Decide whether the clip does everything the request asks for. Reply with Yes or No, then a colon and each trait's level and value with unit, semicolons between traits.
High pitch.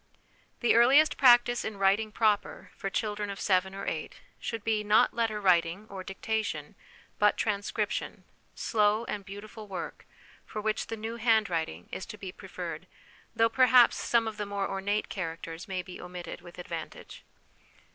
Yes: high, 210 Hz